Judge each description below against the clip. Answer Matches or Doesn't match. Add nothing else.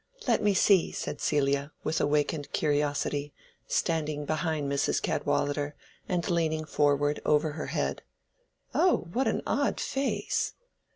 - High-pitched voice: Doesn't match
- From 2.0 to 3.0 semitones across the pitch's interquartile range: Matches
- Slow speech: Matches